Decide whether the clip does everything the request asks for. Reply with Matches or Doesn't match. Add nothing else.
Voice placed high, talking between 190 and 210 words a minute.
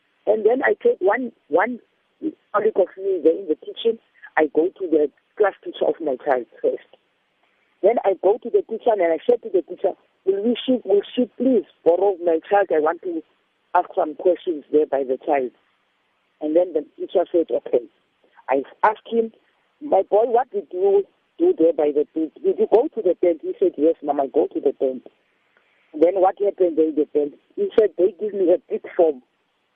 Matches